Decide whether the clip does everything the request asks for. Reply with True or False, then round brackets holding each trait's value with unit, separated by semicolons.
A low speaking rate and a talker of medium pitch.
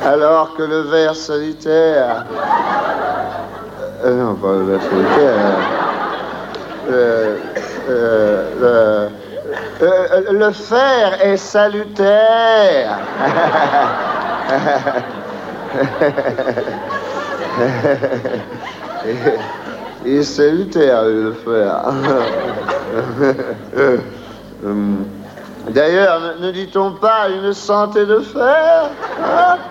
True (60 wpm; 160 Hz)